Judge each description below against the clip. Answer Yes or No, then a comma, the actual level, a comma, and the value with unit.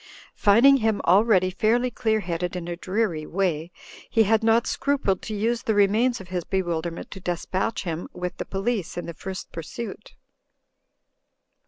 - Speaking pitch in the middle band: No, high, 195 Hz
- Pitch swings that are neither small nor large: Yes, average, 4.1 semitones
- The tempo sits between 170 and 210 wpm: No, average, 160 wpm